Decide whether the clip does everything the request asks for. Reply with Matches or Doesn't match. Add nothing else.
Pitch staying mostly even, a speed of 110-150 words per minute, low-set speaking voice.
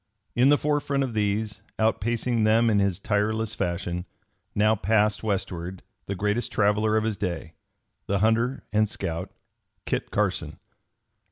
Matches